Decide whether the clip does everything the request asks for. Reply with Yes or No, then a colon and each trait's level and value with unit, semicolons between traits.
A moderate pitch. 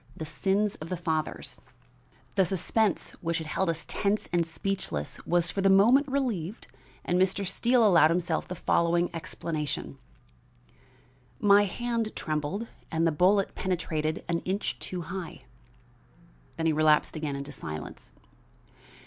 Yes: medium, 175 Hz